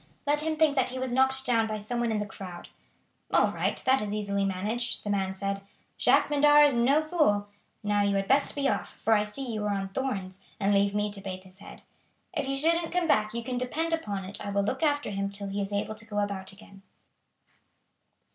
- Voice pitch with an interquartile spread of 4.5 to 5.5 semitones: Yes, average, 5.0 semitones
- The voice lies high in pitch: Yes, high, 215 Hz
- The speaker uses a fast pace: Yes, fast, 230 wpm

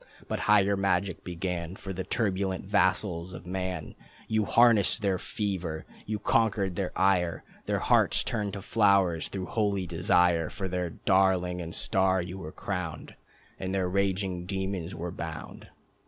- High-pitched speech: No, very low, 95 Hz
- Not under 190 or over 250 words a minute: No, average, 150 wpm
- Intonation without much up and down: Yes, narrow, 1.9 semitones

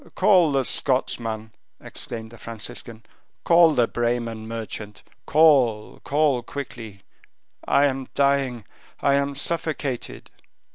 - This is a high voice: No, low, 125 Hz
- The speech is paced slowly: Yes, slow, 105 wpm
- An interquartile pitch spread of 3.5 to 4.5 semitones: Yes, average, 3.8 semitones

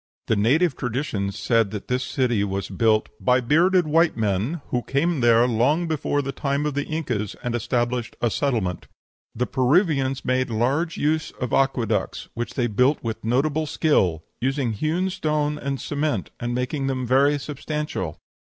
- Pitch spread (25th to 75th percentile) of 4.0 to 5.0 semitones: Yes, average, 4.3 semitones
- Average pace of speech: Yes, average, 160 wpm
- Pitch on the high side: No, low, 130 Hz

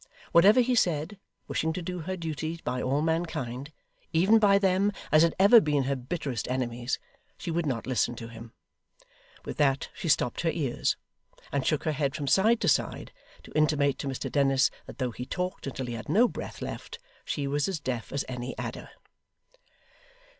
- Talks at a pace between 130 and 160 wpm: No, average, 185 wpm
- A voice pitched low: No, medium, 150 Hz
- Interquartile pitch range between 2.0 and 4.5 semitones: No, average, 5.1 semitones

